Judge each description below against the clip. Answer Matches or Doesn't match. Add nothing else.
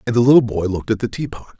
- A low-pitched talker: Matches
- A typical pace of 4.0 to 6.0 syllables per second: Doesn't match